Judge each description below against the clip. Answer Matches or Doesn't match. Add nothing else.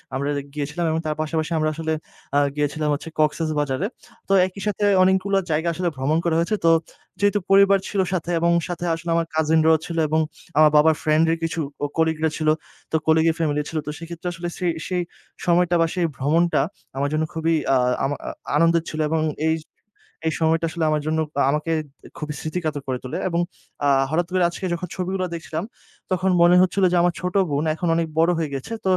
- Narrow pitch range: Matches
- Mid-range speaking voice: Matches